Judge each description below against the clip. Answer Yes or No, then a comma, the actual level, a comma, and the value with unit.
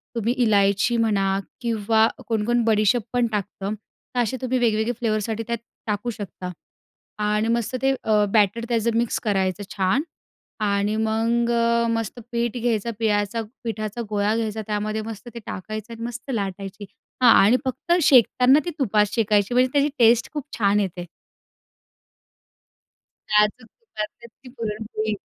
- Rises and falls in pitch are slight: Yes, narrow, 2.1 semitones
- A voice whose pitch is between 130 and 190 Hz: No, high, 220 Hz